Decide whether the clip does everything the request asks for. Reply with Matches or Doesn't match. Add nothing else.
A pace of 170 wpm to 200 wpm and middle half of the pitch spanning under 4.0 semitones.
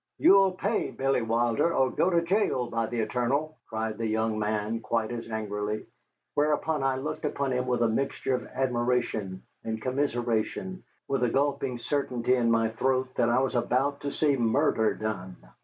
Matches